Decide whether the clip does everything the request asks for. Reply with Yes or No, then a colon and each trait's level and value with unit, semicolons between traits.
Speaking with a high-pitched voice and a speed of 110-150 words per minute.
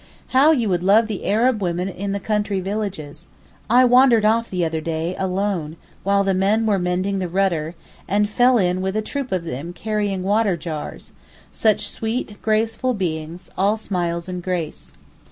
No: high, 195 Hz; average, 170 wpm